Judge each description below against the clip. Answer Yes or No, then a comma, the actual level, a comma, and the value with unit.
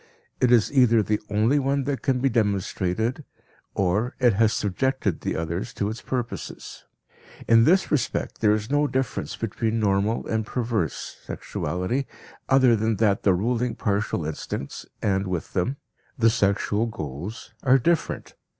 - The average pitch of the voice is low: Yes, low, 110 Hz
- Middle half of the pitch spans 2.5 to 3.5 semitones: No, average, 4.1 semitones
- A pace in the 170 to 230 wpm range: No, average, 150 wpm